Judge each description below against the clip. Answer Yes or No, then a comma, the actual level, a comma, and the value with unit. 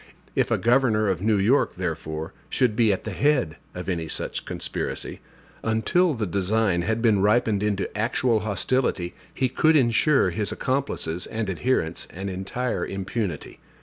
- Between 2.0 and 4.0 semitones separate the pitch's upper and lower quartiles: No, average, 4.6 semitones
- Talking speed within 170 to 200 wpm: No, average, 150 wpm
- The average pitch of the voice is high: No, low, 110 Hz